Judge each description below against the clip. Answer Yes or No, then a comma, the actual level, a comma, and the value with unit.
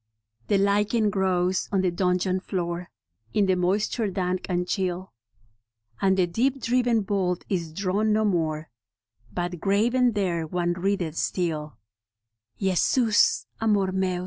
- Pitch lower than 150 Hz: No, medium, 185 Hz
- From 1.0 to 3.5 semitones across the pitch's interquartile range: Yes, narrow, 2.6 semitones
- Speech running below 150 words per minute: Yes, average, 140 wpm